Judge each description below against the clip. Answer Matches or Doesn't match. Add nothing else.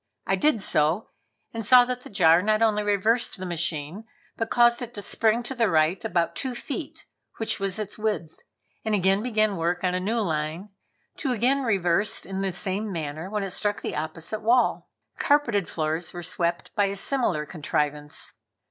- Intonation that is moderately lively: Matches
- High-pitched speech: Matches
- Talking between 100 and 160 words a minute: Doesn't match